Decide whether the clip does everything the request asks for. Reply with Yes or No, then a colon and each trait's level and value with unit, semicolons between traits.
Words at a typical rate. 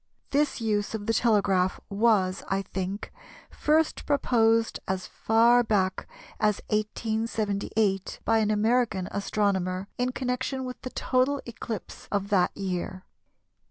No: slow, 125 wpm